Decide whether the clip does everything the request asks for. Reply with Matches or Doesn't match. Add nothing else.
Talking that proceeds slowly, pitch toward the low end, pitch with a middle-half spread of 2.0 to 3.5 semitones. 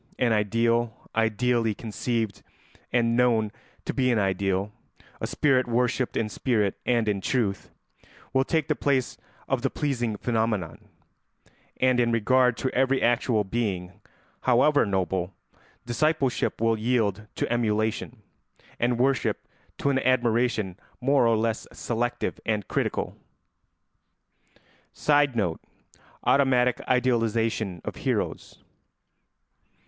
Matches